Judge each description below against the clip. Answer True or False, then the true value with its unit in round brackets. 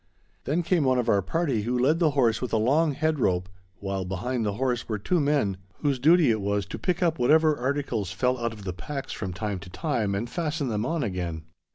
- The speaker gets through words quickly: True (230 wpm)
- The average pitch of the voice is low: True (125 Hz)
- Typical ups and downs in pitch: False (6.5 semitones)